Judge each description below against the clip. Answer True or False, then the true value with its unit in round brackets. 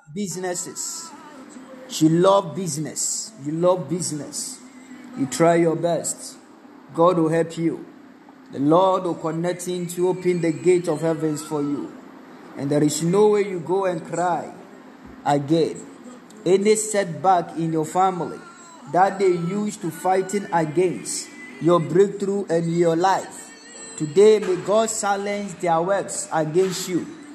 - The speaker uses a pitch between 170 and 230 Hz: True (185 Hz)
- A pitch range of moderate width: True (5.0 semitones)